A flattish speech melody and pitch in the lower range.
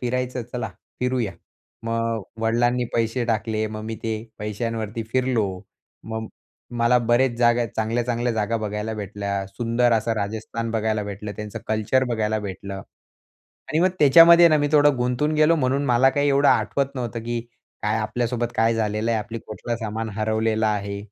Yes: narrow, 2.3 semitones; low, 115 Hz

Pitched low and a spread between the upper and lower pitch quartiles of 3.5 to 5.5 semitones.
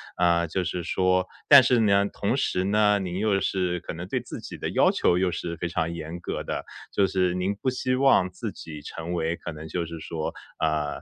No: very low, 90 Hz; average, 2.8 semitones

